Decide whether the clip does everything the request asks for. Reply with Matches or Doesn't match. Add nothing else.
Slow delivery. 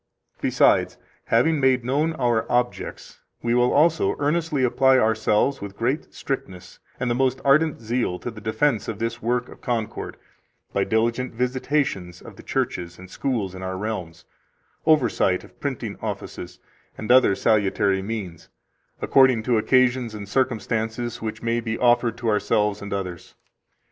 Doesn't match